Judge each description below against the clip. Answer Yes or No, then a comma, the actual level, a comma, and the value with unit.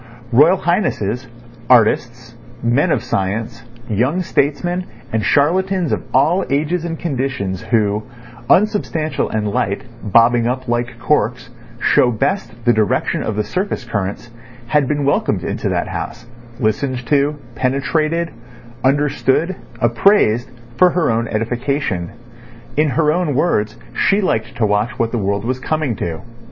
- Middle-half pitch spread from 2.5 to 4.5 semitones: No, average, 5.2 semitones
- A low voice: Yes, low, 125 Hz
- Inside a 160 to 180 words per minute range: No, slow, 135 wpm